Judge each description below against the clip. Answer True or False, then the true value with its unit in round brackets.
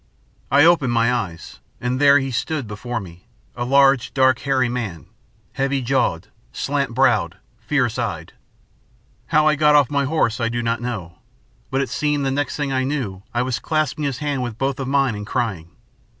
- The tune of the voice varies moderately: True (3.1 semitones)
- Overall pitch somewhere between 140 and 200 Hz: False (130 Hz)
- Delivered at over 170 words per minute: True (185 wpm)